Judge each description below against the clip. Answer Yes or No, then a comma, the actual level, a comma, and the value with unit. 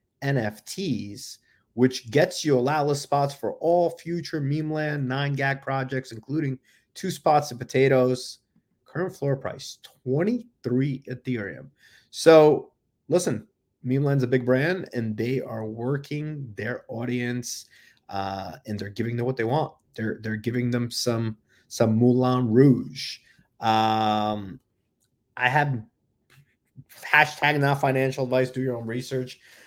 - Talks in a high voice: No, low, 130 Hz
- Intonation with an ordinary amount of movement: Yes, average, 3.2 semitones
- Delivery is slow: Yes, slow, 130 wpm